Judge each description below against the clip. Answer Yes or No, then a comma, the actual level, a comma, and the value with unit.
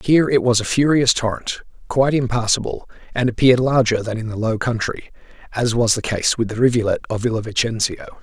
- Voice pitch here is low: Yes, low, 120 Hz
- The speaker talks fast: No, average, 190 wpm